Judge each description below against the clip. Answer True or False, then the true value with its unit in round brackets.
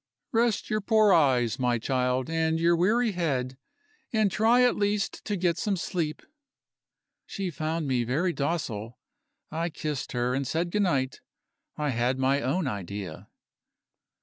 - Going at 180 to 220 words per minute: False (150 wpm)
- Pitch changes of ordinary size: False (6.5 semitones)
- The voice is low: False (160 Hz)